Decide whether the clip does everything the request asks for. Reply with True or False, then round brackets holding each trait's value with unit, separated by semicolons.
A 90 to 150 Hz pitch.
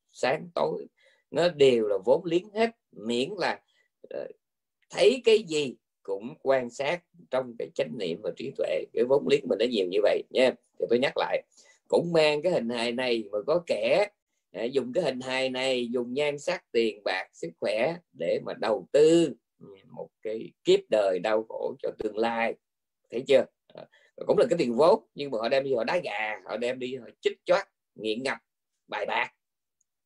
False (210 Hz)